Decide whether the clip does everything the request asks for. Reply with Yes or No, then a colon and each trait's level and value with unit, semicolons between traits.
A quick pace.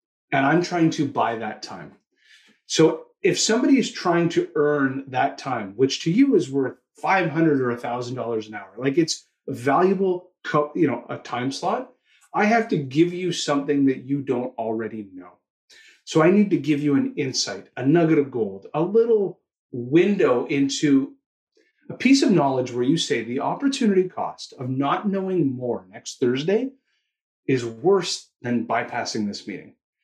No: average, 170 wpm